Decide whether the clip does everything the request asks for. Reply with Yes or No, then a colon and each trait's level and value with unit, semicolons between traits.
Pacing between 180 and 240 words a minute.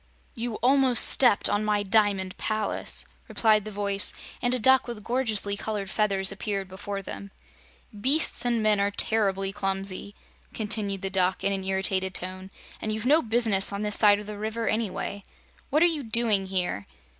No: average, 170 wpm